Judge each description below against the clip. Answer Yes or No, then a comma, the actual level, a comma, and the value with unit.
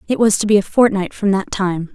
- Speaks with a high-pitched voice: Yes, high, 200 Hz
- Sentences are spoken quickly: Yes, fast, 280 wpm